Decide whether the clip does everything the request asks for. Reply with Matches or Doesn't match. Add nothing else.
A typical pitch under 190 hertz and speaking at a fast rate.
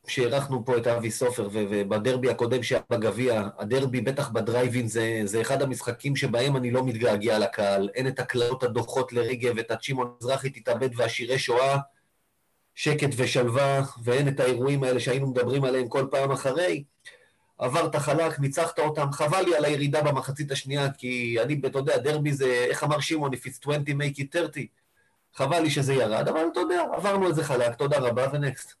Matches